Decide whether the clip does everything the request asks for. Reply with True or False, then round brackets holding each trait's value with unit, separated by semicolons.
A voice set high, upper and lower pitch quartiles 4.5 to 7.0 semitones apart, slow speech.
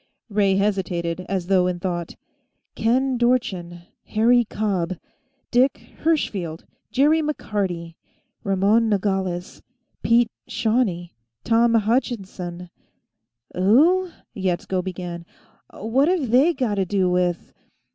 True (200 Hz; 5.0 semitones; 100 wpm)